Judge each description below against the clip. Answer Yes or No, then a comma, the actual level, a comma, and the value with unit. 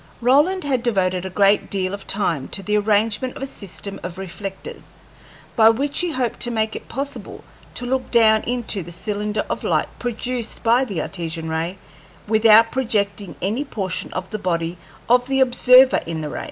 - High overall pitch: Yes, high, 215 Hz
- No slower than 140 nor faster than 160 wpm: No, average, 180 wpm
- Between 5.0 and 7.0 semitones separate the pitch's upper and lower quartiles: No, average, 4.4 semitones